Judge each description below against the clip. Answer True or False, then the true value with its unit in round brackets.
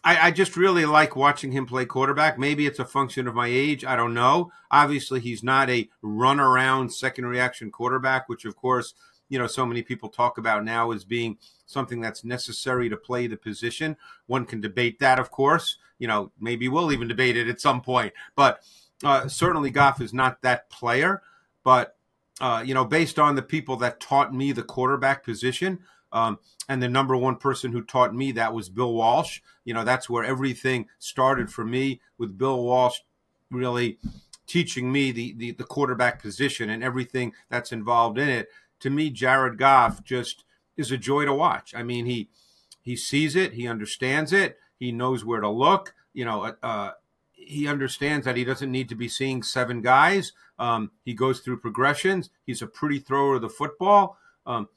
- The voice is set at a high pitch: False (130 Hz)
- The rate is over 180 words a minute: True (190 wpm)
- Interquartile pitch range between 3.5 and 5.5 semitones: False (2.5 semitones)